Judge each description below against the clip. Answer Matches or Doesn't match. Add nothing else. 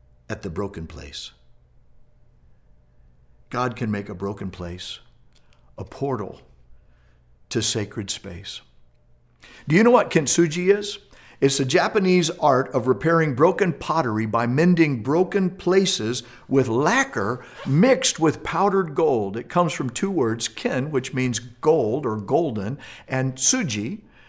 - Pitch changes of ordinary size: Doesn't match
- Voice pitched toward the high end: Doesn't match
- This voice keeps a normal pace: Doesn't match